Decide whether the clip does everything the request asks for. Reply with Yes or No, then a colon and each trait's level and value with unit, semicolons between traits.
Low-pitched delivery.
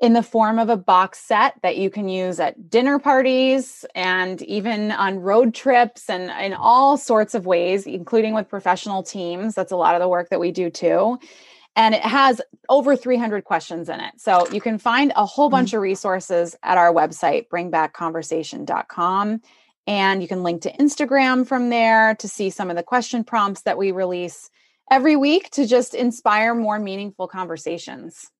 No: high, 210 Hz